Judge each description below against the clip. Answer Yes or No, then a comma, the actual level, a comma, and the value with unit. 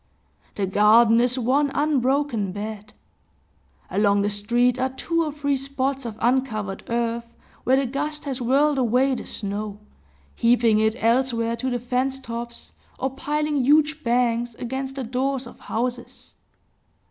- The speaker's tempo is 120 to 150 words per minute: Yes, average, 145 wpm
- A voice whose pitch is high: Yes, high, 245 Hz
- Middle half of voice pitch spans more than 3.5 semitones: No, average, 2.9 semitones